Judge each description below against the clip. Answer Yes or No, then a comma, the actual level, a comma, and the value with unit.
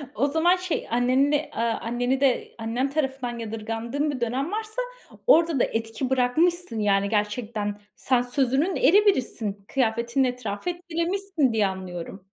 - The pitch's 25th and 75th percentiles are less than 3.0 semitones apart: No, wide, 5.6 semitones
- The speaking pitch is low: No, very high, 250 Hz